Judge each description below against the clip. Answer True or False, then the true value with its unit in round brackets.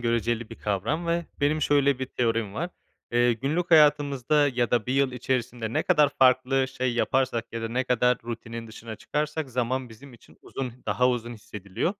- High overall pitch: False (125 Hz)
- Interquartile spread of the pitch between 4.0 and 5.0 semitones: False (3.3 semitones)